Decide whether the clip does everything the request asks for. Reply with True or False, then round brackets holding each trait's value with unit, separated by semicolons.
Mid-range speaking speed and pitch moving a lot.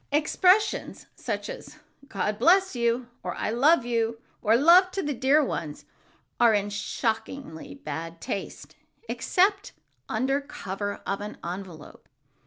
False (130 wpm; 6.6 semitones)